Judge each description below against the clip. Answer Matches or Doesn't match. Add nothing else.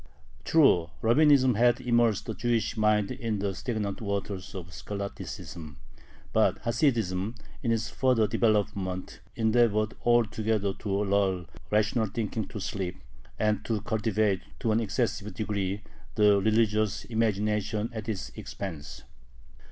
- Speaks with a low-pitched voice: Matches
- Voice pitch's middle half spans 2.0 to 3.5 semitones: Matches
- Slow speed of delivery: Matches